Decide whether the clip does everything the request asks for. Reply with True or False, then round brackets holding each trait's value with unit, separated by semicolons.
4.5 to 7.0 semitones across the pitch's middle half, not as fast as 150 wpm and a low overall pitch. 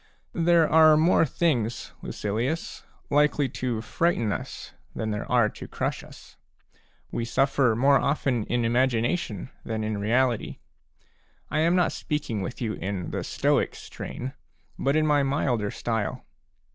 True (4.9 semitones; 140 wpm; 125 Hz)